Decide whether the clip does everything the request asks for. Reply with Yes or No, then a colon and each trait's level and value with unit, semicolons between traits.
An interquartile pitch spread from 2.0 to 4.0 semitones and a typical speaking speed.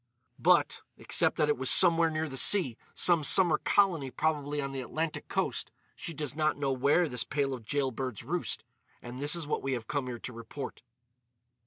Yes: average, 3.4 semitones; average, 180 wpm